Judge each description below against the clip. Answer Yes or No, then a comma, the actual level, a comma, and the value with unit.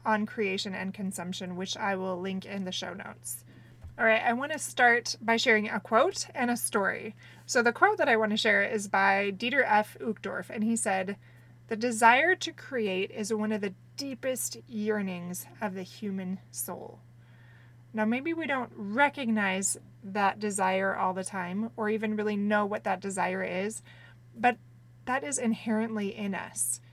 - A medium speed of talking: Yes, average, 175 wpm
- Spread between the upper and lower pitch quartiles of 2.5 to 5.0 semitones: Yes, average, 3.4 semitones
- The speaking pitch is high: Yes, high, 205 Hz